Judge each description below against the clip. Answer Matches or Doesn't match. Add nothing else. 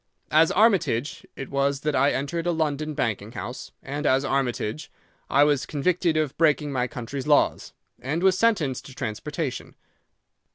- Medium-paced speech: Matches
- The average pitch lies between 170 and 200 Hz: Doesn't match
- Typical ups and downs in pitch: Matches